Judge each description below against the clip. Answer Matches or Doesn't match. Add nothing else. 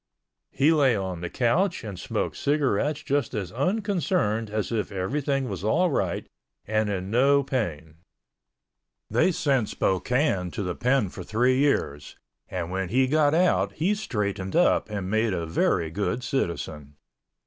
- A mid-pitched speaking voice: Doesn't match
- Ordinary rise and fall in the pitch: Doesn't match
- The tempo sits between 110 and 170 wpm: Matches